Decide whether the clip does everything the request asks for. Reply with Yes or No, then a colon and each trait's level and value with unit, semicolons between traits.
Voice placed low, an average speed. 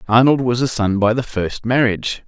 No: low, 115 Hz; fast, 210 wpm